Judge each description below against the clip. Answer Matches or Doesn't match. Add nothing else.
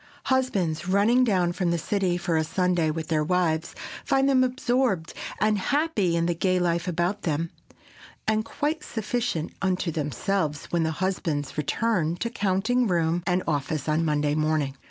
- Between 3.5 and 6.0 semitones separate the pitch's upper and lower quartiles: Matches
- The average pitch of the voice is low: Doesn't match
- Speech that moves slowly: Doesn't match